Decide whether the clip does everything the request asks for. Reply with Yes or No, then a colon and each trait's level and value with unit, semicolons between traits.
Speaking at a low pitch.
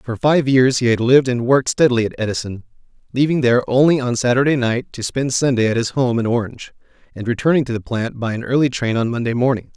Yes: low, 125 Hz